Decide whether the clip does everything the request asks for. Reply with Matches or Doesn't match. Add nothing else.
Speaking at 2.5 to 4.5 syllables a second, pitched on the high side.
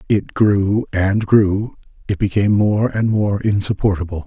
Doesn't match